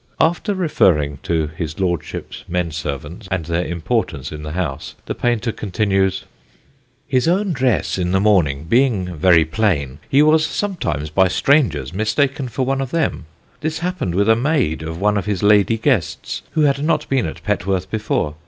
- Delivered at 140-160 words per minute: No, average, 170 wpm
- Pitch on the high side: No, low, 100 Hz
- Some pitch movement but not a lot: No, wide, 8.3 semitones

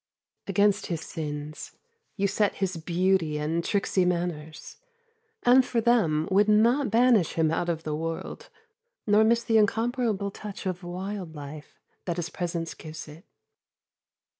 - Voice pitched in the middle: Yes, medium, 180 Hz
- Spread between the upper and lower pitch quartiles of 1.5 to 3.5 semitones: No, average, 4.5 semitones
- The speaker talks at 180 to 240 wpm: No, average, 140 wpm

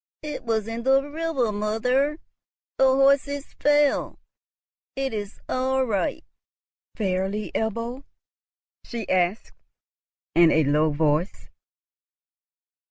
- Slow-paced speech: Yes, slow, 100 wpm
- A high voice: Yes, high, 230 Hz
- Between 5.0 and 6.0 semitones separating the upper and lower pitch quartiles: Yes, wide, 5.6 semitones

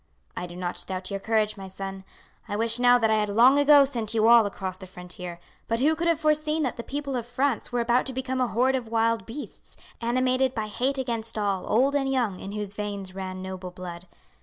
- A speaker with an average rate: No, fast, 230 wpm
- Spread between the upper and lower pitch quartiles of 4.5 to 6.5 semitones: Yes, average, 4.9 semitones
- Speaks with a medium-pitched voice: No, high, 230 Hz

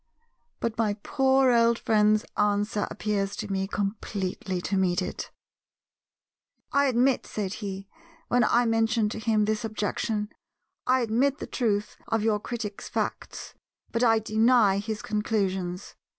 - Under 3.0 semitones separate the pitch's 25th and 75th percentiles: Yes, narrow, 2.4 semitones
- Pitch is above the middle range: Yes, high, 215 Hz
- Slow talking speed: Yes, slow, 130 wpm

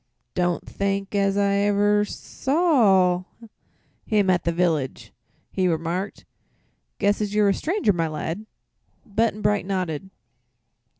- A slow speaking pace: Yes, slow, 120 wpm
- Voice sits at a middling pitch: No, high, 200 Hz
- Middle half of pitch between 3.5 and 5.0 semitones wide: No, narrow, 2.6 semitones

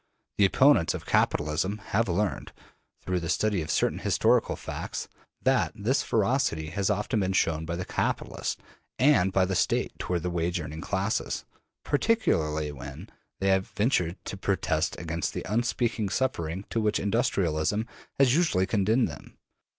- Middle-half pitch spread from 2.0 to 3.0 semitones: No, average, 4.8 semitones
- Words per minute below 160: Yes, average, 150 wpm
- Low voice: Yes, very low, 95 Hz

